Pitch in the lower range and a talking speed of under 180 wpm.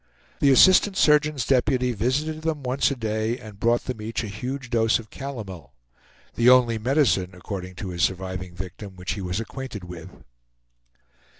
Yes: low, 115 Hz; average, 165 wpm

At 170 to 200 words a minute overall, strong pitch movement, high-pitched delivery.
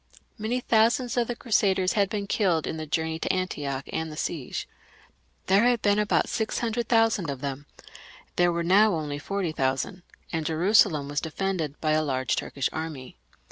No: average, 180 wpm; wide, 5.7 semitones; medium, 175 Hz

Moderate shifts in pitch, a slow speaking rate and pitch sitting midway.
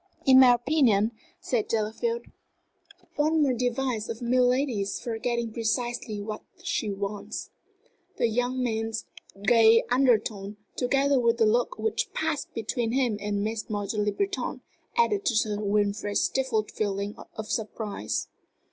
No: average, 3.2 semitones; slow, 130 wpm; high, 230 Hz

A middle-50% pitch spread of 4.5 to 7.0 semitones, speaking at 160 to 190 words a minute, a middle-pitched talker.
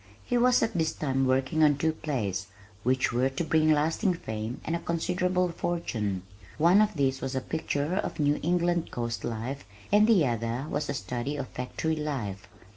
Yes: average, 5.0 semitones; average, 185 wpm; medium, 145 Hz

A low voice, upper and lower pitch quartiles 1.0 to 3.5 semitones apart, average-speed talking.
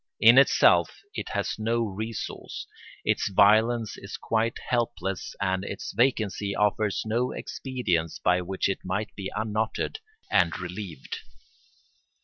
No: low, 105 Hz; average, 3.0 semitones; slow, 125 wpm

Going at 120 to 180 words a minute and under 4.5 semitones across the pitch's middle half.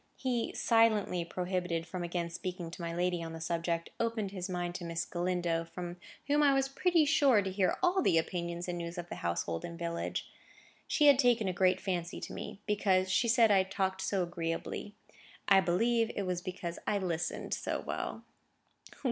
No: average, 190 wpm; average, 3.5 semitones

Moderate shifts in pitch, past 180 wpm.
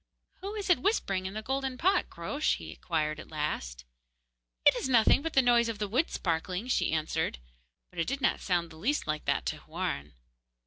No: wide, 8.8 semitones; fast, 205 wpm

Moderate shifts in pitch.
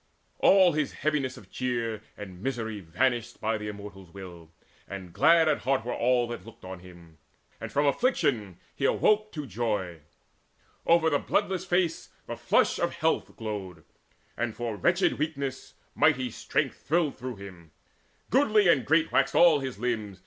No: wide, 7.3 semitones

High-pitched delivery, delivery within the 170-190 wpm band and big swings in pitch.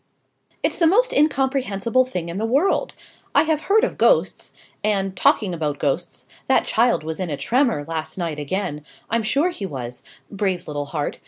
Yes: high, 195 Hz; average, 175 wpm; wide, 8.9 semitones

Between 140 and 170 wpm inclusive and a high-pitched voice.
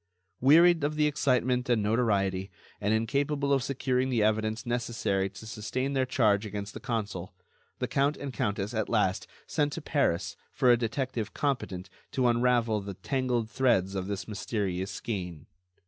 No: average, 160 wpm; low, 115 Hz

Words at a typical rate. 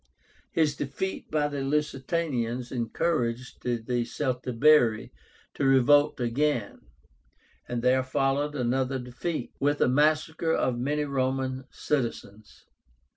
No: slow, 105 wpm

